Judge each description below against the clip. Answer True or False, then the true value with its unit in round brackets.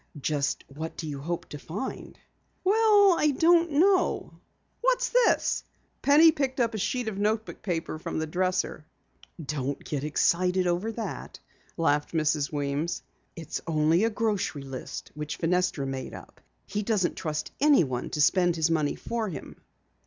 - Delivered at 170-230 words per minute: False (150 wpm)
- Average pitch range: False (7.4 semitones)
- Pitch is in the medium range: True (175 Hz)